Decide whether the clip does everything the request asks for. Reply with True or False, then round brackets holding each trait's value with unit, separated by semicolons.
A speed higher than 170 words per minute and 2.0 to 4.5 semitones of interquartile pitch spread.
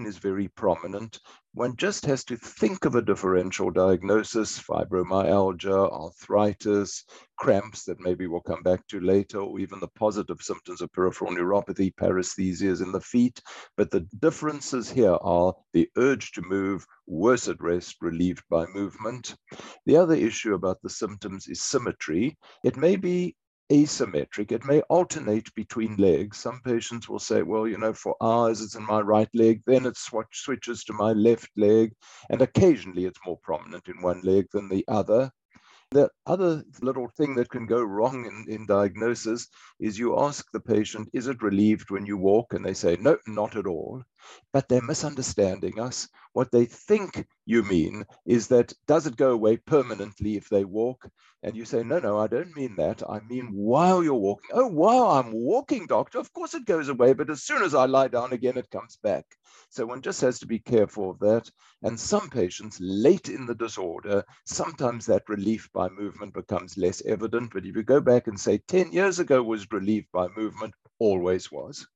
True (185 wpm; 4.1 semitones)